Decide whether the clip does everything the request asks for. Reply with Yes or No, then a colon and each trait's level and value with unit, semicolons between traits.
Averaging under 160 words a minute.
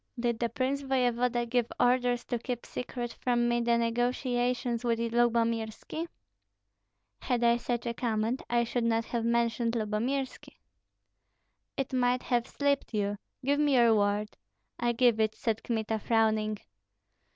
Yes: average, 140 wpm